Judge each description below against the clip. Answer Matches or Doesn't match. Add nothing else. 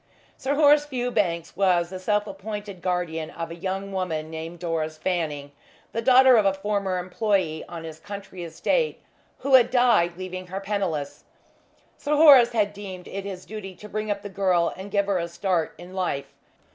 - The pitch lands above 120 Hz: Matches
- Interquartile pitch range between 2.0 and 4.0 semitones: Matches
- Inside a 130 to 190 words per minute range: Matches